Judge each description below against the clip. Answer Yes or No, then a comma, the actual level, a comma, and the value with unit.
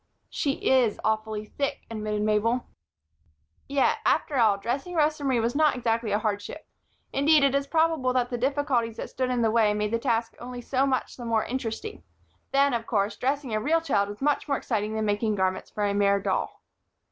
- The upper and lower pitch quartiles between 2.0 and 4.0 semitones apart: No, average, 4.4 semitones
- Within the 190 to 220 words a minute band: Yes, average, 195 wpm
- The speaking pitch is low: No, high, 235 Hz